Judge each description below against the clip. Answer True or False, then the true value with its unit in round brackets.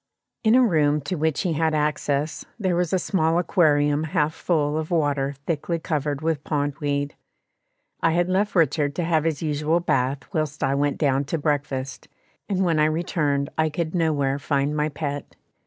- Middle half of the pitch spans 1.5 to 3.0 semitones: True (2.4 semitones)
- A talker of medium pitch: True (155 Hz)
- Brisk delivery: False (180 wpm)